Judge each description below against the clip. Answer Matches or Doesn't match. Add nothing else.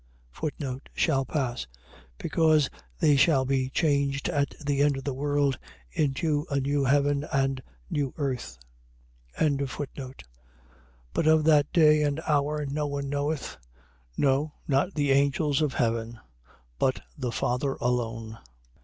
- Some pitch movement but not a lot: Doesn't match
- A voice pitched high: Doesn't match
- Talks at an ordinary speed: Doesn't match